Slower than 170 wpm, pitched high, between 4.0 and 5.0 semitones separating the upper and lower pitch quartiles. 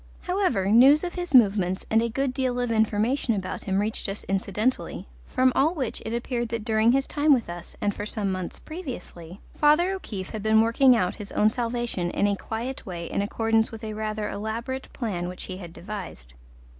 No: average, 200 wpm; high, 220 Hz; average, 4.3 semitones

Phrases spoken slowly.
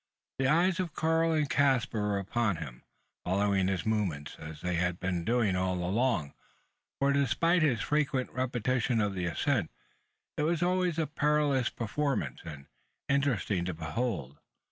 No: average, 150 wpm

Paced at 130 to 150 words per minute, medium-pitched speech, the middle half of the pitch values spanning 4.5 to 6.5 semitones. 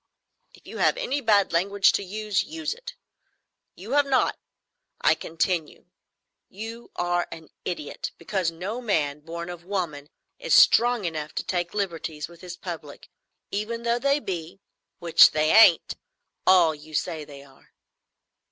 Yes: average, 145 wpm; medium, 180 Hz; wide, 5.4 semitones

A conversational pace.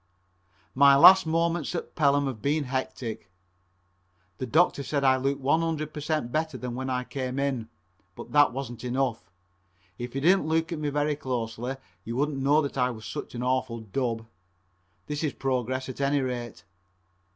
Yes: average, 175 wpm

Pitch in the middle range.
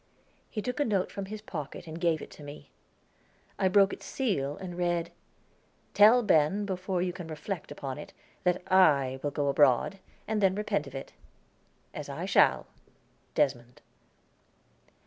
Yes: medium, 175 Hz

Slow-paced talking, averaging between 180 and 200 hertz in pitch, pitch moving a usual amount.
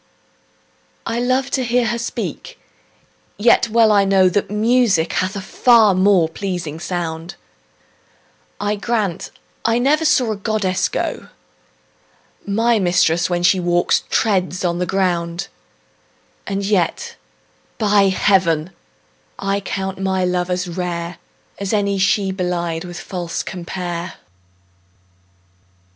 Yes: slow, 120 wpm; high, 190 Hz; average, 3.1 semitones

